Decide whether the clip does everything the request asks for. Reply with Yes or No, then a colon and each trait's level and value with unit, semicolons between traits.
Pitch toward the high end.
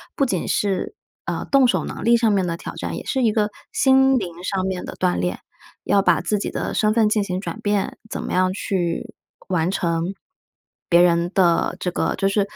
Yes: high, 195 Hz